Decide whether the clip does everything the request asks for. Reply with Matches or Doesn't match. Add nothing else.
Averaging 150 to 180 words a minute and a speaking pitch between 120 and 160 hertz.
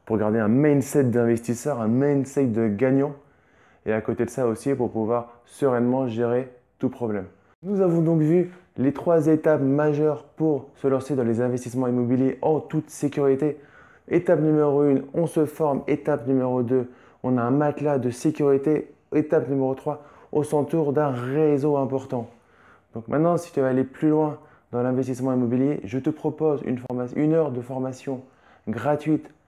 Matches